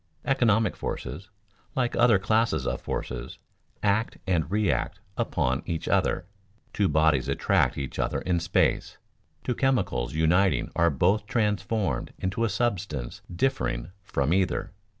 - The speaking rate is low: Yes, slow, 130 wpm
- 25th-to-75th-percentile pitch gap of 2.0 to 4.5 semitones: No, wide, 5.6 semitones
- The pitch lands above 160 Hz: No, very low, 95 Hz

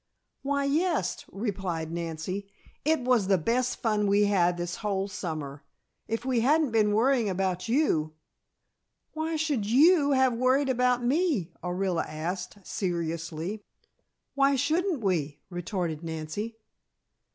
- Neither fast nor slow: No, slow, 130 wpm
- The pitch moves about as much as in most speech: No, wide, 6.9 semitones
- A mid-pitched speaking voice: No, high, 210 Hz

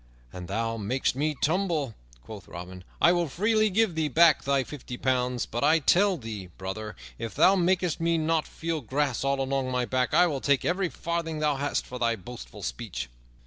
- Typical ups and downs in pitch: No, wide, 6.0 semitones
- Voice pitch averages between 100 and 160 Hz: Yes, medium, 140 Hz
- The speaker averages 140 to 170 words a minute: No, average, 190 wpm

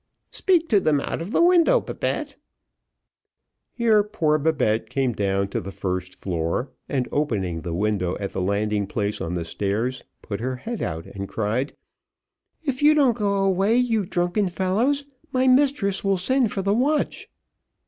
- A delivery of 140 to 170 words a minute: Yes, average, 165 wpm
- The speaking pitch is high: No, medium, 155 Hz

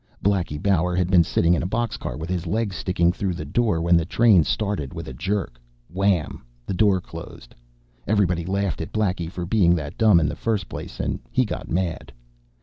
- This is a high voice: No, very low, 90 Hz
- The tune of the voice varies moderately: Yes, average, 3.2 semitones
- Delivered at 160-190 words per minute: No, average, 200 wpm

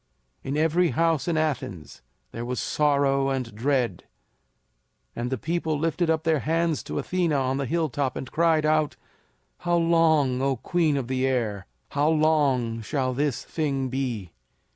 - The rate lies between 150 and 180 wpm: Yes, average, 155 wpm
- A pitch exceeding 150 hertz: No, medium, 140 Hz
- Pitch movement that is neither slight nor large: Yes, average, 3.8 semitones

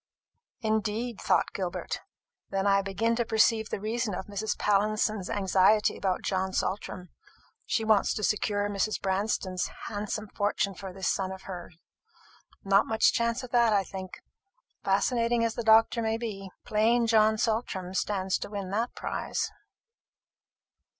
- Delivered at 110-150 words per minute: Yes, average, 145 wpm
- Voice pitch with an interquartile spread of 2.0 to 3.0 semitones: Yes, narrow, 2.5 semitones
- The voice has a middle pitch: No, high, 210 Hz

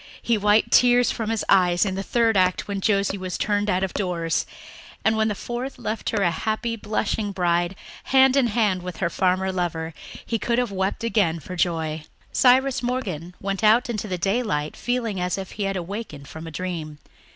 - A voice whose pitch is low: No, high, 195 Hz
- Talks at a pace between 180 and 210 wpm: Yes, average, 195 wpm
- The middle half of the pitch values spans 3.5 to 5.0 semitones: Yes, average, 4.0 semitones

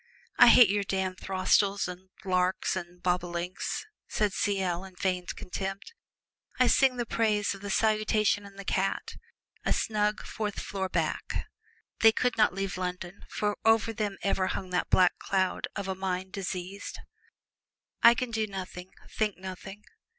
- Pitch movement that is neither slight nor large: No, narrow, 2.2 semitones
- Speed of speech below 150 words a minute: No, average, 160 wpm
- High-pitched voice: Yes, high, 195 Hz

